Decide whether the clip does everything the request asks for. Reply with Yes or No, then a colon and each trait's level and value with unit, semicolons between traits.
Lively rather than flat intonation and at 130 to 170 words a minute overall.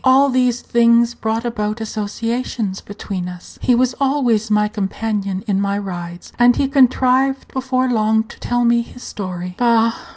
No: average, 3.3 semitones; average, 160 wpm